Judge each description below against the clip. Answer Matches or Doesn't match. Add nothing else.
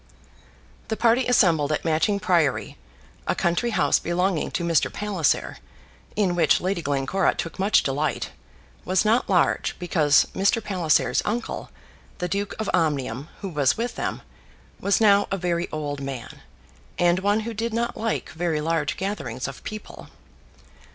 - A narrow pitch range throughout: Doesn't match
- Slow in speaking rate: Doesn't match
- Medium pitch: Matches